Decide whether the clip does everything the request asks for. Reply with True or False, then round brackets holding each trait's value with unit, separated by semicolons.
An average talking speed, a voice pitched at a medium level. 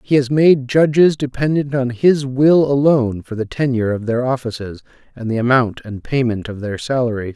False (190 wpm; 125 Hz)